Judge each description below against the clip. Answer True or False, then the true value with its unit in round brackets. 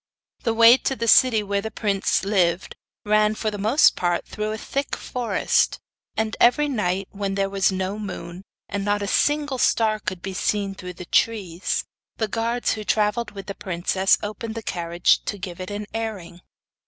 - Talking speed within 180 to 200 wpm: True (185 wpm)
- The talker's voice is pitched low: False (205 Hz)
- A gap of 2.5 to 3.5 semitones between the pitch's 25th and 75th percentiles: True (2.9 semitones)